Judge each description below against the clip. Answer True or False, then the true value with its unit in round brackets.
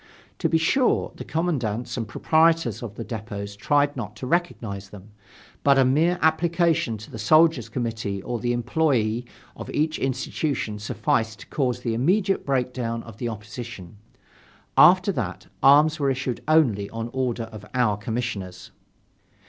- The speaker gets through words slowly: False (150 wpm)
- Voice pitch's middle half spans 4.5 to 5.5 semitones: True (5.1 semitones)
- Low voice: True (120 Hz)